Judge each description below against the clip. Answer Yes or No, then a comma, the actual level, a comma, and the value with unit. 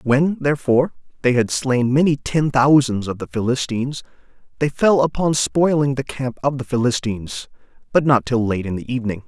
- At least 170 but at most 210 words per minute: Yes, average, 175 wpm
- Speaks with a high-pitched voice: No, low, 130 Hz